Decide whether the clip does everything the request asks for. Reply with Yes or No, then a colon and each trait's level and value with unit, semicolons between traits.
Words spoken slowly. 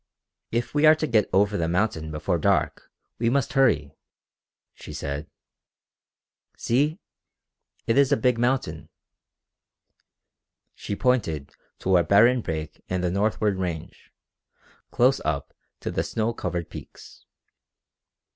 Yes: slow, 125 wpm